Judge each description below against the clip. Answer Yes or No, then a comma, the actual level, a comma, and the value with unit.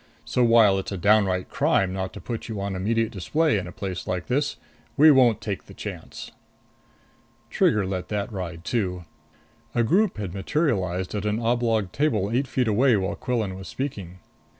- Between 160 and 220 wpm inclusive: Yes, average, 175 wpm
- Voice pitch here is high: No, low, 105 Hz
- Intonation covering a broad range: No, average, 4.2 semitones